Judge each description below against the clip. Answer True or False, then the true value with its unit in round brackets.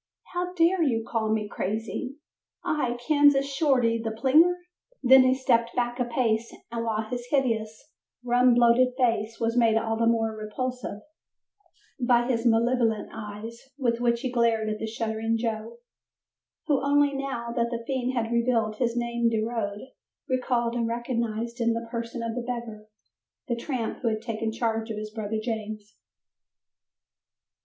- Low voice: False (235 Hz)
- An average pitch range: False (2.1 semitones)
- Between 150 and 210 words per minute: True (160 wpm)